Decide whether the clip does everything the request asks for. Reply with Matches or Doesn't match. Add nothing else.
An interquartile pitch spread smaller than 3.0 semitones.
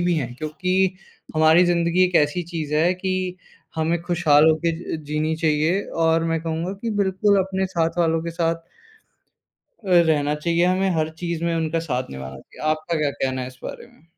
Matches